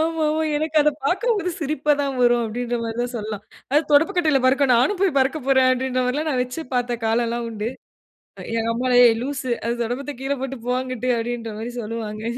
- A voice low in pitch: No, very high, 255 Hz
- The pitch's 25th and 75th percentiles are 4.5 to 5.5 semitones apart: No, average, 3.7 semitones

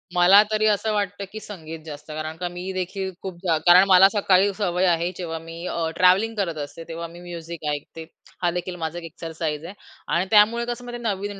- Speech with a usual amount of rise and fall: Yes, average, 3.4 semitones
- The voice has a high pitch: No, medium, 180 Hz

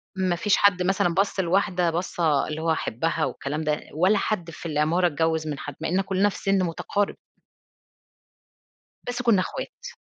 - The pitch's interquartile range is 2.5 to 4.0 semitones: Yes, average, 3.4 semitones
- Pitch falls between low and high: Yes, medium, 175 Hz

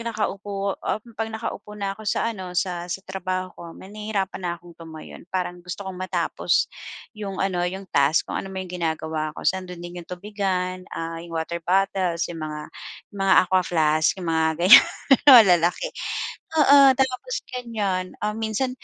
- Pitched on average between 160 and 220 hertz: Yes, medium, 185 Hz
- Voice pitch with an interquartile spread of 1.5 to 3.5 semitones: Yes, average, 2.9 semitones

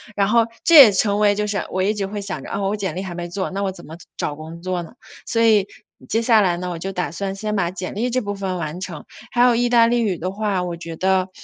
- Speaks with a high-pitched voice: Yes, high, 195 Hz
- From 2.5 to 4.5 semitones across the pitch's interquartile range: Yes, average, 2.8 semitones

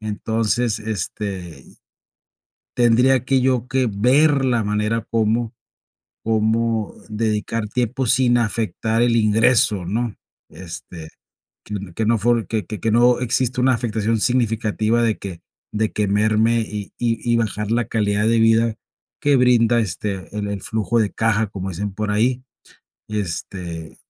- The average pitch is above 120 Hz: No, low, 110 Hz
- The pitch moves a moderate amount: No, narrow, 2.2 semitones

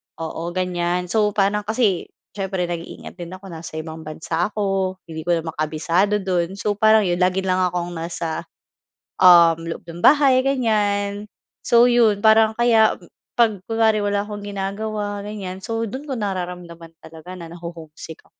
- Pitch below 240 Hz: Yes, high, 190 Hz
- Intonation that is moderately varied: Yes, average, 3.5 semitones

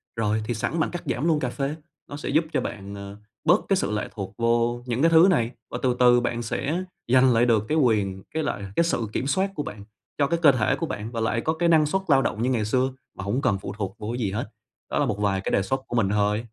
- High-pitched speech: No, low, 120 Hz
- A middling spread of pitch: No, wide, 5.7 semitones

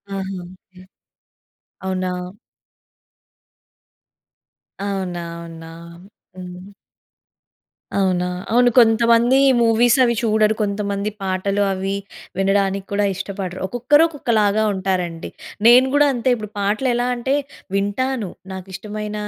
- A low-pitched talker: No, high, 200 Hz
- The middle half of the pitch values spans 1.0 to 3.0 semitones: No, average, 3.7 semitones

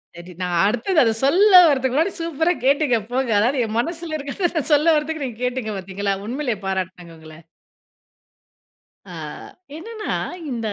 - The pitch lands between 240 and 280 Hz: Yes, very high, 260 Hz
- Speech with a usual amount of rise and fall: No, wide, 7.4 semitones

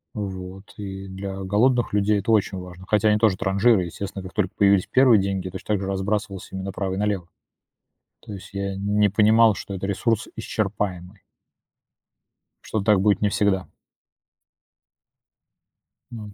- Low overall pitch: Yes, low, 100 Hz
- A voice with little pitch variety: Yes, narrow, 1.8 semitones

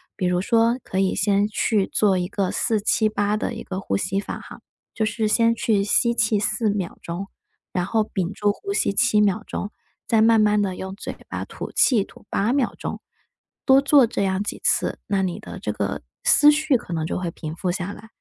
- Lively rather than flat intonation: No, average, 3.0 semitones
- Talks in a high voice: Yes, high, 210 Hz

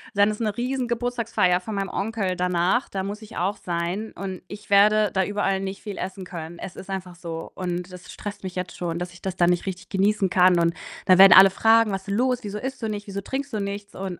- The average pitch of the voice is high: Yes, high, 195 Hz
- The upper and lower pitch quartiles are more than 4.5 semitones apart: No, average, 2.7 semitones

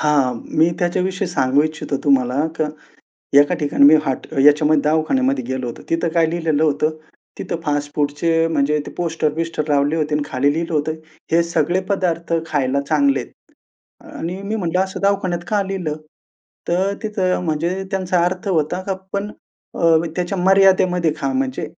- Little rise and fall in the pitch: No, average, 3.7 semitones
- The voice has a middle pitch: Yes, medium, 165 Hz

